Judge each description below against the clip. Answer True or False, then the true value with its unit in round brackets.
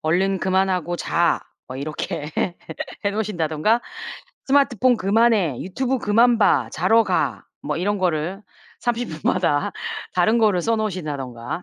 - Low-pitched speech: False (190 Hz)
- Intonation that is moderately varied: False (5.8 semitones)